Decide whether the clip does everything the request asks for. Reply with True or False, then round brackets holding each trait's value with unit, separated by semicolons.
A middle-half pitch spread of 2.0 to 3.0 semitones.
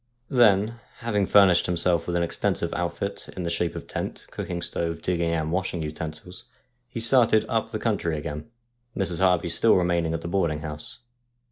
True (2.7 semitones)